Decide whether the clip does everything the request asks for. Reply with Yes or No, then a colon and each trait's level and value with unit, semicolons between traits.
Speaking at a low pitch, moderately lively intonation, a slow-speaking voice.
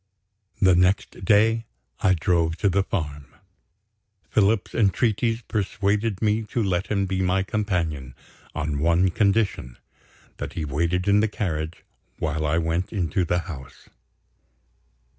Yes: very low, 95 Hz; average, 4.0 semitones; slow, 130 wpm